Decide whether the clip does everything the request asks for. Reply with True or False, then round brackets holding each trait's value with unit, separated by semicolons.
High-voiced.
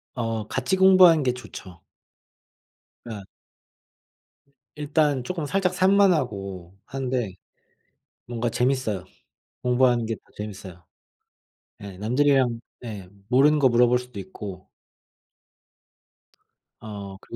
False (125 Hz)